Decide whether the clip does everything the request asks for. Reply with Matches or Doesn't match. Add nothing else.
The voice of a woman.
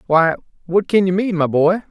Doesn't match